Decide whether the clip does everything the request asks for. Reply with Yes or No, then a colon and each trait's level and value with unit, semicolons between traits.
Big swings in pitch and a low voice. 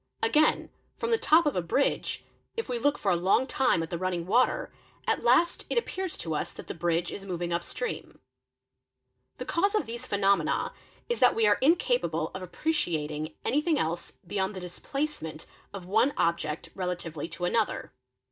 No: wide, 9.0 semitones; high, 195 Hz